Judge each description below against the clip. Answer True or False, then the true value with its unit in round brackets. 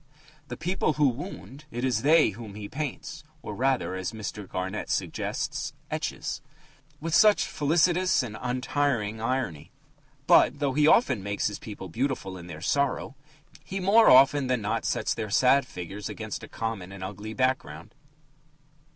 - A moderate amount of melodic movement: False (5.9 semitones)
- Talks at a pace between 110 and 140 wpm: False (155 wpm)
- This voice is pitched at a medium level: False (125 Hz)